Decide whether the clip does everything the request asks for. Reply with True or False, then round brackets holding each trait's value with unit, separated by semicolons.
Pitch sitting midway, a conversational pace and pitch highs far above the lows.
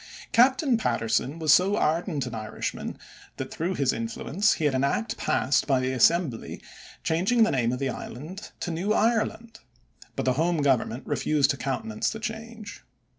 True (160 Hz; 170 wpm; 8.6 semitones)